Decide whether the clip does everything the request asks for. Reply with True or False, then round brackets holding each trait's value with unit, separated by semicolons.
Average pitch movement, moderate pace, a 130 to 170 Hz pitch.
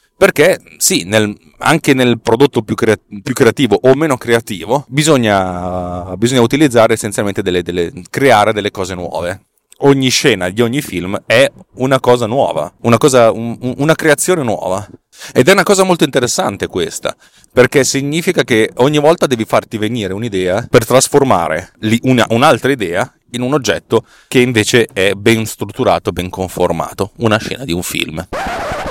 False (4.6 semitones; 155 wpm; 115 Hz)